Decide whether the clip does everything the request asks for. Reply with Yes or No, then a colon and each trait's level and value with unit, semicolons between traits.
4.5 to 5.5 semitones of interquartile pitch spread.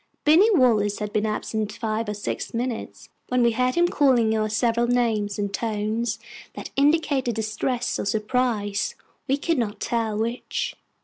No: average, 3.0 semitones